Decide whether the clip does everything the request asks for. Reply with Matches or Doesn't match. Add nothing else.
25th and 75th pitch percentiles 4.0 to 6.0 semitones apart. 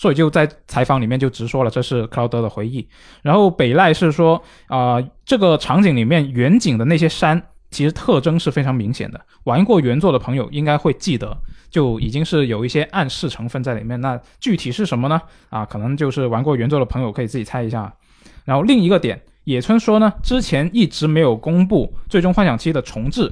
Matches